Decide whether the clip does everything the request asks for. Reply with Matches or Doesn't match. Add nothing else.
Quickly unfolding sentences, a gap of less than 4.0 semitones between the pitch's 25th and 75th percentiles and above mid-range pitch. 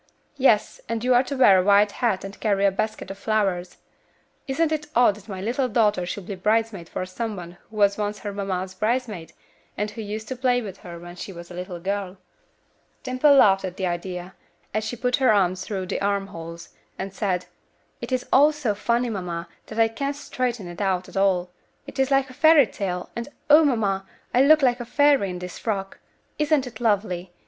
Doesn't match